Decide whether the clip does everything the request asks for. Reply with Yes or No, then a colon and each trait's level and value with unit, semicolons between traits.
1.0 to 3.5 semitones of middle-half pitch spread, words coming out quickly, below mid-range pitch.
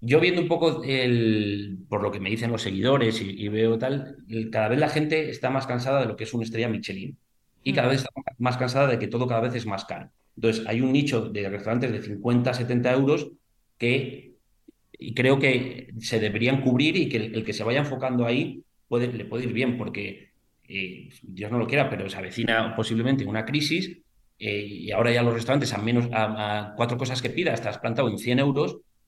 Yes: average, 3.1 semitones; fast, 220 wpm; low, 120 Hz